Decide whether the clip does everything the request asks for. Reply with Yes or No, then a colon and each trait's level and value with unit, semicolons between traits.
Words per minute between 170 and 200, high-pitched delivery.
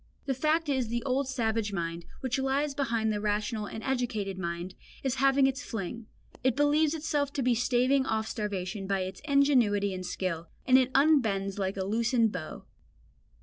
Yes: average, 180 wpm; high, 235 Hz